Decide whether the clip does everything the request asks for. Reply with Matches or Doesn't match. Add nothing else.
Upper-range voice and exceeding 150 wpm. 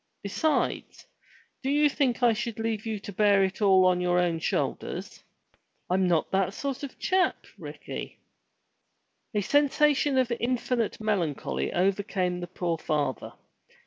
Doesn't match